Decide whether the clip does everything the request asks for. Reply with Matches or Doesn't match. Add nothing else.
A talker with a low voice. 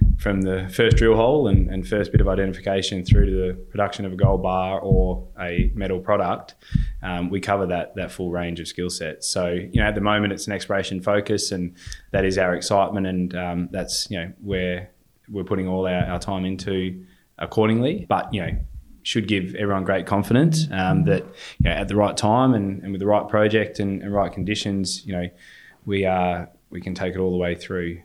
Matches